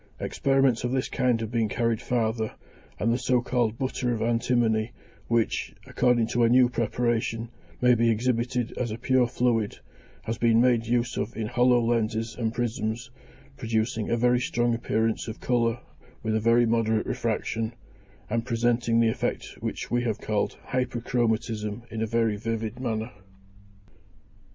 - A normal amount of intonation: No, narrow, 1.5 semitones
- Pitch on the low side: Yes, low, 115 Hz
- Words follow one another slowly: No, average, 155 wpm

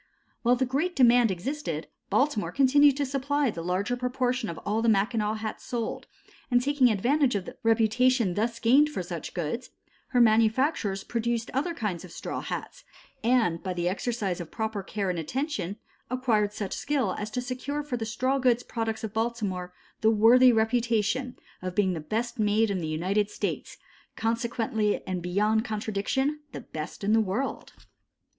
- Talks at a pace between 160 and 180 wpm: Yes, average, 170 wpm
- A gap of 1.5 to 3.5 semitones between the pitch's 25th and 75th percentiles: No, average, 3.9 semitones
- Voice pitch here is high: Yes, high, 225 Hz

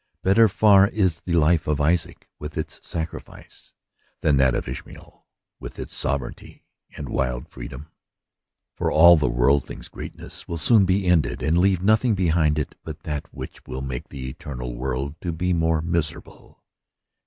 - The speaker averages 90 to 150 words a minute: No, average, 165 wpm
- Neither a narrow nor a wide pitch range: Yes, average, 4.5 semitones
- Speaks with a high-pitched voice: No, very low, 80 Hz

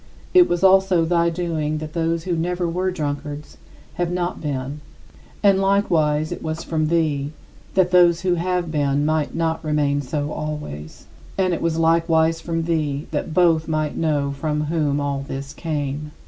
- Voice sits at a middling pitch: Yes, medium, 160 Hz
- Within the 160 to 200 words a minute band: Yes, average, 165 wpm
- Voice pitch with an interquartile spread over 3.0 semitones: No, narrow, 2.5 semitones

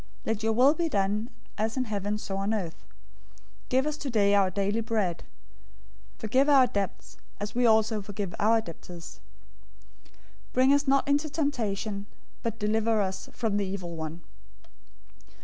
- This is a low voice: No, high, 215 Hz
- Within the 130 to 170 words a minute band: Yes, average, 165 wpm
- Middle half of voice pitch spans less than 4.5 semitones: Yes, average, 3.9 semitones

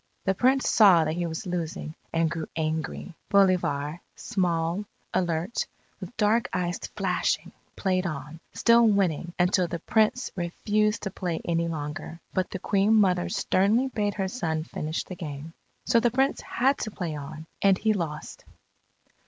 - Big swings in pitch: No, average, 4.2 semitones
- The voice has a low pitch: No, medium, 180 Hz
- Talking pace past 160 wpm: No, average, 155 wpm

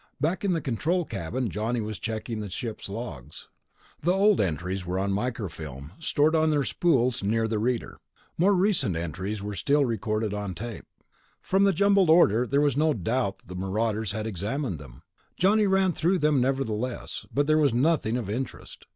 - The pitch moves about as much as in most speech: No, wide, 7.3 semitones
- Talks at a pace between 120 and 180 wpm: Yes, average, 175 wpm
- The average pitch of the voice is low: Yes, low, 115 Hz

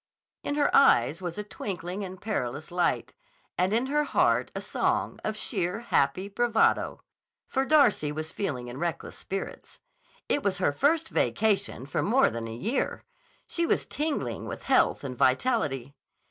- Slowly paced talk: No, average, 160 wpm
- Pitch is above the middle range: Yes, high, 195 Hz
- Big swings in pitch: Yes, wide, 8.4 semitones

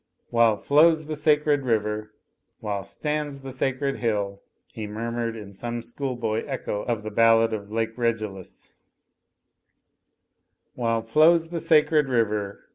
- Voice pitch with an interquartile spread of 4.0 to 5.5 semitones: Yes, average, 4.7 semitones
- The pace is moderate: No, slow, 125 wpm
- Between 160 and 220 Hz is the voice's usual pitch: No, low, 115 Hz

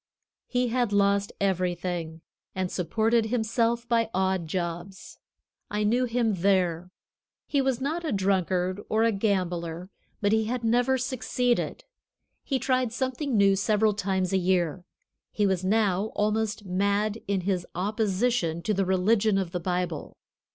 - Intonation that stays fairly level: No, average, 3.8 semitones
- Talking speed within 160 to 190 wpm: No, average, 145 wpm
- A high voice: Yes, high, 200 Hz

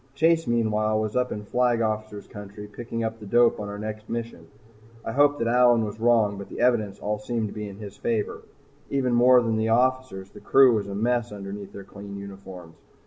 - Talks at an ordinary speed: No, fast, 210 wpm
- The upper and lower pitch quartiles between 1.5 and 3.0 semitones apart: Yes, average, 2.7 semitones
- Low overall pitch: Yes, low, 110 Hz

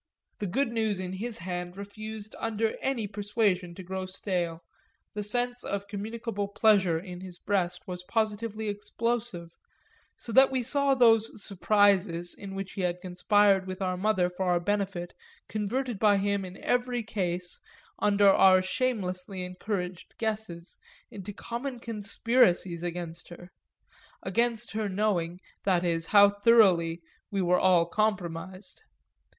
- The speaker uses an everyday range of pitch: Yes, average, 3.4 semitones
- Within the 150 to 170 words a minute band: No, average, 140 wpm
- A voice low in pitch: No, high, 200 Hz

